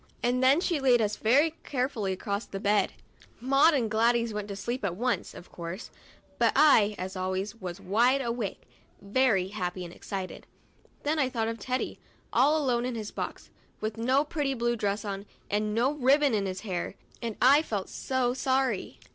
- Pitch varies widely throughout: No, average, 4.5 semitones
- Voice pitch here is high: Yes, high, 230 Hz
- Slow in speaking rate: No, average, 180 wpm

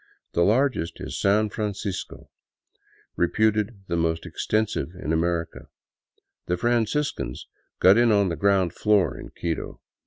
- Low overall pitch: Yes, low, 100 Hz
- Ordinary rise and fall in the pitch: Yes, average, 4.0 semitones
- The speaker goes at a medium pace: No, slow, 130 wpm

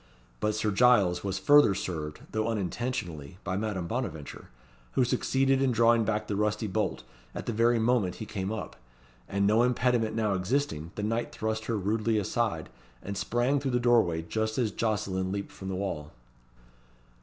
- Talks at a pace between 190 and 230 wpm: No, average, 170 wpm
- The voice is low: Yes, low, 110 Hz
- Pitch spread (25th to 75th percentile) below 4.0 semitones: Yes, average, 3.6 semitones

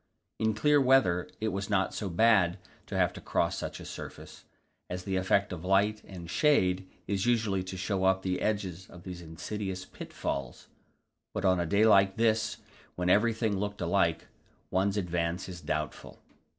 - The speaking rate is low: No, average, 170 wpm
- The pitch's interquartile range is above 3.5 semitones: No, average, 2.8 semitones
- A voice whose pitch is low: Yes, very low, 95 Hz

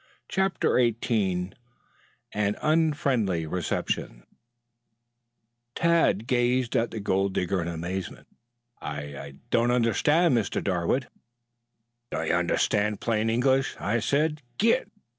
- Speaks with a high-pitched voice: No, low, 115 Hz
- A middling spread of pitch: No, wide, 5.8 semitones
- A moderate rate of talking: No, slow, 105 wpm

